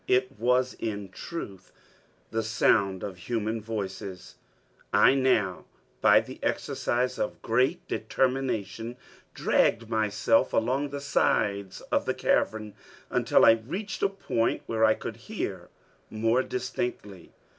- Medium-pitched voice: No, low, 115 Hz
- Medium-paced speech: No, slow, 125 wpm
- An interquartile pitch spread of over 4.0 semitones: No, average, 3.7 semitones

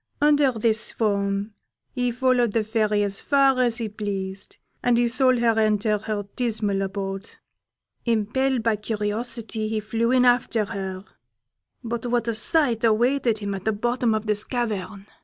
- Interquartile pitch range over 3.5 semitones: No, average, 2.7 semitones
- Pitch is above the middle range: Yes, high, 220 Hz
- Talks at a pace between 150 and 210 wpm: Yes, average, 160 wpm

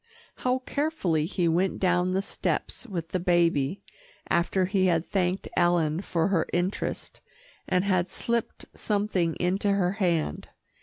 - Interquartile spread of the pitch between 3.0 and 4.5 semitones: No, narrow, 2.5 semitones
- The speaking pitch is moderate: Yes, medium, 180 Hz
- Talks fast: No, average, 140 wpm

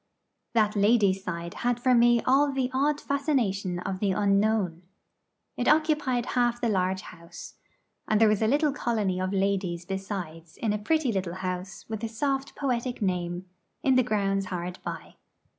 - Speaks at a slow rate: No, average, 165 wpm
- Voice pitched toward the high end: Yes, high, 210 Hz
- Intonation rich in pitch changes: No, average, 4.9 semitones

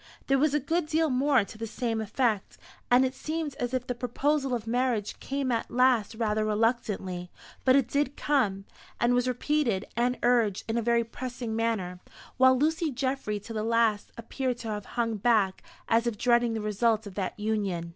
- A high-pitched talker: Yes, high, 235 Hz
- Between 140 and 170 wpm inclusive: No, average, 190 wpm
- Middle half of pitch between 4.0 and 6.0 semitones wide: No, average, 3.2 semitones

